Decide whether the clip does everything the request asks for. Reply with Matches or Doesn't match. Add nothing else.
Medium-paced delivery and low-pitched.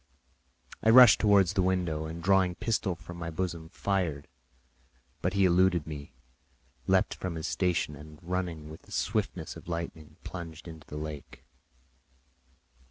Matches